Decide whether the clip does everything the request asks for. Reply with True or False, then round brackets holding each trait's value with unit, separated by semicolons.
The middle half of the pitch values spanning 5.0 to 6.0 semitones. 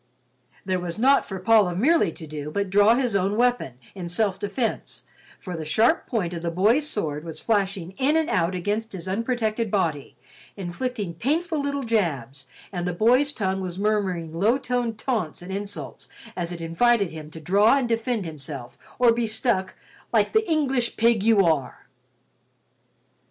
True (5.5 semitones)